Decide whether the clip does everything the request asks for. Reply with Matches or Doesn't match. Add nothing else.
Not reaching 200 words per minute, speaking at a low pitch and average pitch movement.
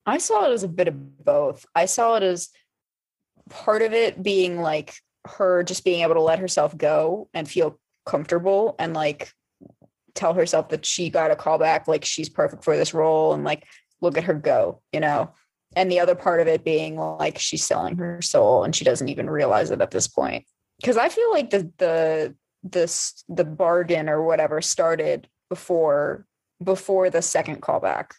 Doesn't match